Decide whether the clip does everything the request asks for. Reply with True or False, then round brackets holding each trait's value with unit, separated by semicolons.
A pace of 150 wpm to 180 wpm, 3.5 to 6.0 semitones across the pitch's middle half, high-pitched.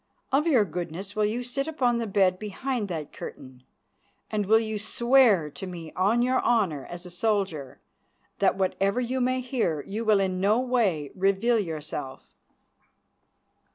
True (155 wpm; 5.2 semitones; 205 Hz)